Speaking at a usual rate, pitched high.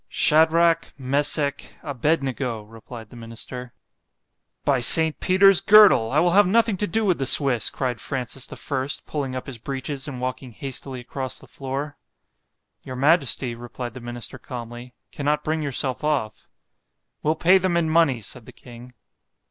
No: average, 155 wpm; low, 135 Hz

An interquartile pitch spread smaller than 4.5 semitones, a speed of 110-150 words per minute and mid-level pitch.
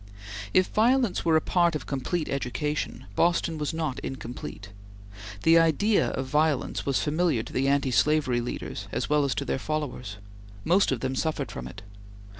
No: average, 4.1 semitones; average, 170 wpm; medium, 150 Hz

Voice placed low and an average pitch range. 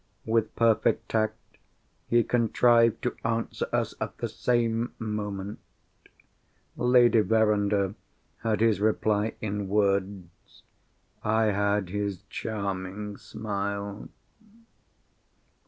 No: low, 105 Hz; narrow, 2.0 semitones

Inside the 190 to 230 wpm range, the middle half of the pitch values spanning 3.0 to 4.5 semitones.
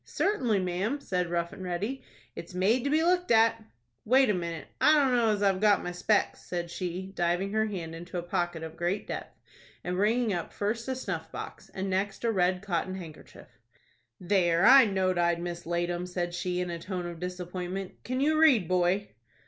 Yes: average, 195 wpm; average, 3.8 semitones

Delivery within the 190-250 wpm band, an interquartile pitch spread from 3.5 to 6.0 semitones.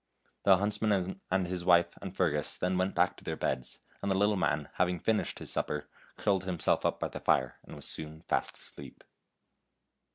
No: average, 200 wpm; average, 3.1 semitones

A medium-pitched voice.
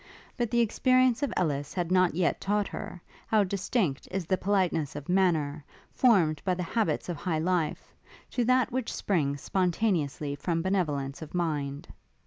Yes: medium, 180 Hz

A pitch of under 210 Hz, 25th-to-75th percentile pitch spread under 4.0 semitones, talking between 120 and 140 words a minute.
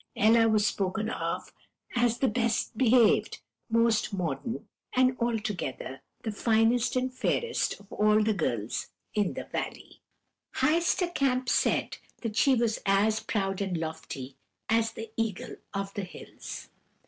No: high, 220 Hz; average, 3.3 semitones; slow, 135 wpm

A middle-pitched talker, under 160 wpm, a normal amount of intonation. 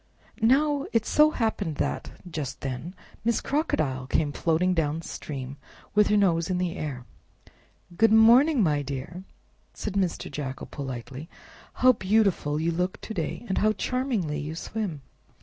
No: medium, 180 Hz; average, 150 wpm; wide, 7.0 semitones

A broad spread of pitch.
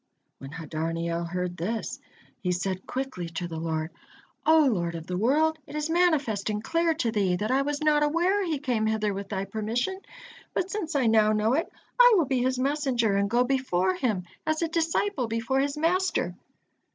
Yes: wide, 8.2 semitones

